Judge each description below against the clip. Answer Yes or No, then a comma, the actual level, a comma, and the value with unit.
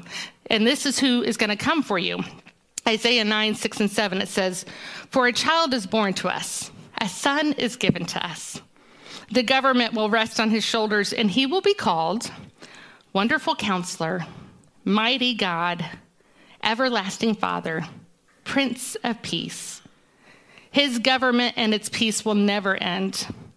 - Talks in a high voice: Yes, high, 225 Hz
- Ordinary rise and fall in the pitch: Yes, average, 3.7 semitones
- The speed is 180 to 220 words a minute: No, average, 150 wpm